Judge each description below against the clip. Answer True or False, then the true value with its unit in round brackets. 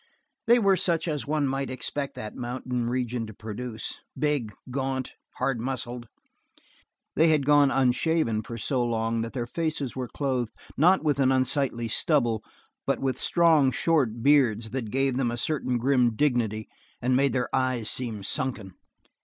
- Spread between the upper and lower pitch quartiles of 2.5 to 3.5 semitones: True (3.1 semitones)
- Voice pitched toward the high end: False (130 Hz)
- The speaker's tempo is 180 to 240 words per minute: False (160 wpm)